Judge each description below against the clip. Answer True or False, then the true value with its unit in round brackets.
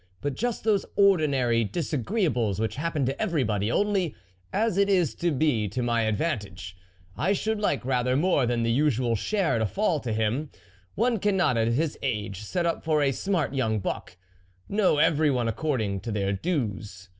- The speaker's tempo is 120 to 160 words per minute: False (180 wpm)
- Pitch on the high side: False (135 Hz)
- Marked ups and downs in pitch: True (7.6 semitones)